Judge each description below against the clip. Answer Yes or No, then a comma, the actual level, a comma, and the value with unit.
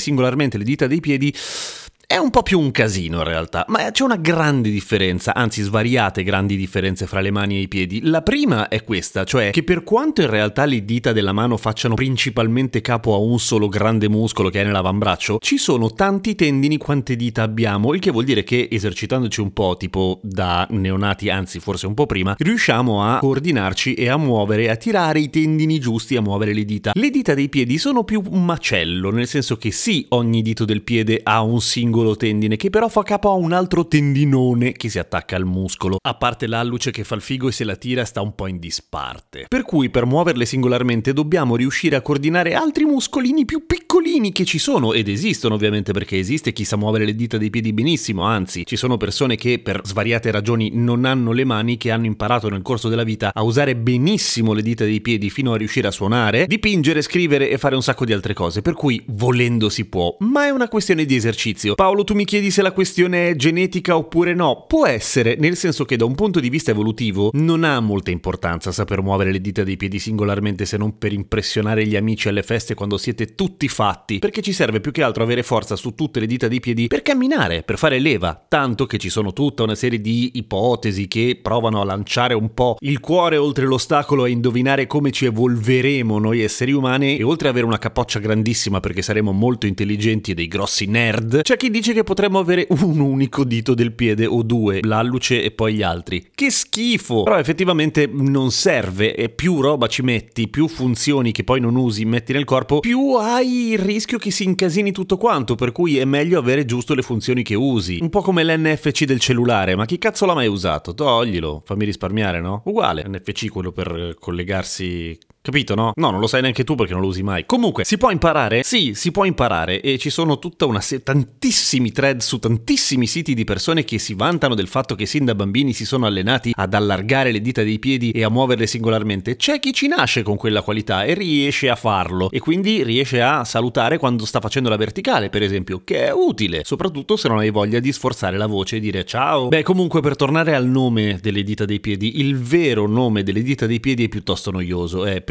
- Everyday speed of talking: No, fast, 215 wpm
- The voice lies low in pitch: Yes, low, 120 Hz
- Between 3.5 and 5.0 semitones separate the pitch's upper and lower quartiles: No, wide, 5.6 semitones